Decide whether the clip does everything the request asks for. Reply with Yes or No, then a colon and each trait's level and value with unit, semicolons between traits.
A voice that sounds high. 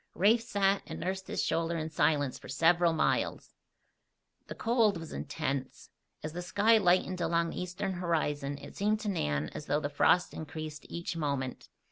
No: medium, 170 Hz